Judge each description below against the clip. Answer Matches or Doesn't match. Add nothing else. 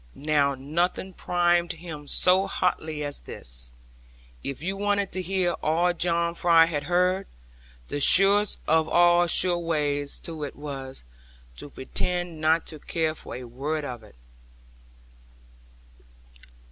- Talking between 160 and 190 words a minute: Doesn't match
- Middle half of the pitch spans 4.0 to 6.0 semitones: Doesn't match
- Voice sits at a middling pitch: Matches